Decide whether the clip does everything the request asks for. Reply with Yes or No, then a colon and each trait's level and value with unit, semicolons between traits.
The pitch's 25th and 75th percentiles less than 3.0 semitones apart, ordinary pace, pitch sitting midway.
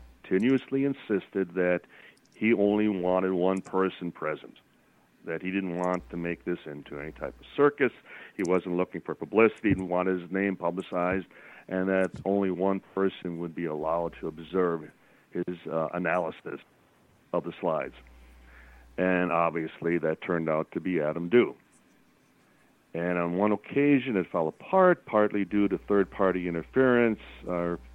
No: narrow, 2.5 semitones; average, 150 wpm; very low, 90 Hz